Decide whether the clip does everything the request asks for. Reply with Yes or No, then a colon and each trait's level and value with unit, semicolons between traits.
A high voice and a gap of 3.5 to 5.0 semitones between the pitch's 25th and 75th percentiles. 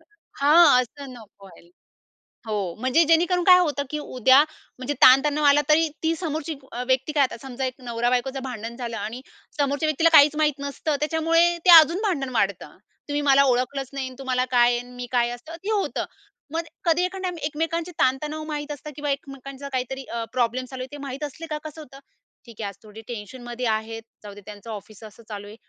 Yes: very high, 270 Hz; average, 4.0 semitones